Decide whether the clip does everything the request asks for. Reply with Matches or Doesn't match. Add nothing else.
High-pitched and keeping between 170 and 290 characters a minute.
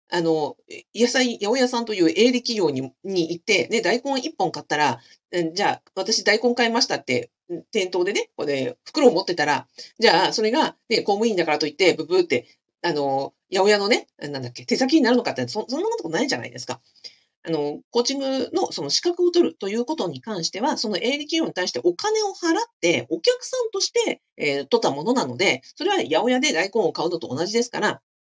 Doesn't match